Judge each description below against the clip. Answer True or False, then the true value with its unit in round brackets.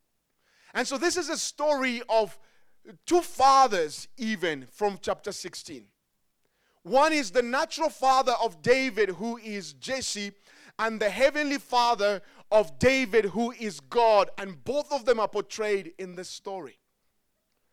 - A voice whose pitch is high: True (230 Hz)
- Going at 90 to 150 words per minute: True (140 wpm)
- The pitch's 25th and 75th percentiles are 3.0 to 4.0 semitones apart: False (4.7 semitones)